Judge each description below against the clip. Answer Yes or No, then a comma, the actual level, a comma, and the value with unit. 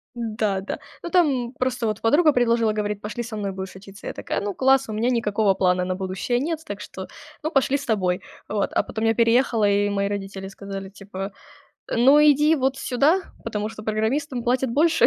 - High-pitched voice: Yes, high, 220 Hz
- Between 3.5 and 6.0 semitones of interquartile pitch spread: Yes, average, 4.5 semitones